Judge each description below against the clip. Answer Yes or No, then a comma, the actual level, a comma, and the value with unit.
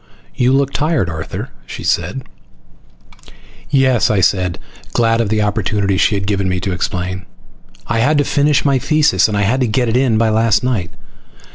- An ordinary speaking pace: Yes, average, 165 wpm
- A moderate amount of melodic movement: Yes, average, 5.0 semitones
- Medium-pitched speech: No, low, 110 Hz